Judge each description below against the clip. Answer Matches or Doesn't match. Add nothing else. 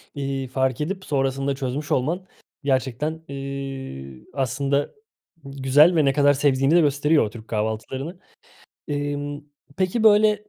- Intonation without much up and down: Matches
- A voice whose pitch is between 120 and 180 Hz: Matches